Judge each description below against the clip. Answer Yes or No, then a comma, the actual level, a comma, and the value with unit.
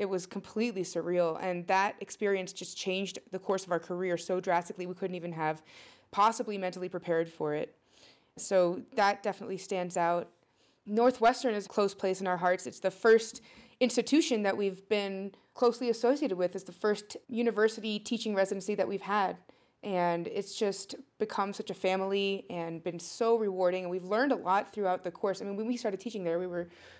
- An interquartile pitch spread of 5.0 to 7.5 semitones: No, average, 3.0 semitones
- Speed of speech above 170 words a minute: Yes, average, 190 wpm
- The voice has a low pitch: No, high, 195 Hz